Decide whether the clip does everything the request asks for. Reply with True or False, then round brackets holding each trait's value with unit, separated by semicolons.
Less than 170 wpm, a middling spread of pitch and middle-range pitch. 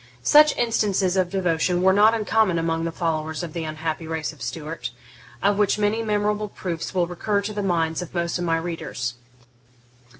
False (180 wpm; 4.0 semitones; 175 Hz)